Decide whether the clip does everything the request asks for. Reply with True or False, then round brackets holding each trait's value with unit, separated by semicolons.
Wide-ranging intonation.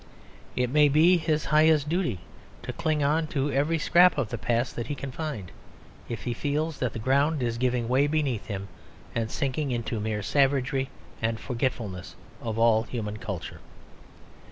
False (4.6 semitones)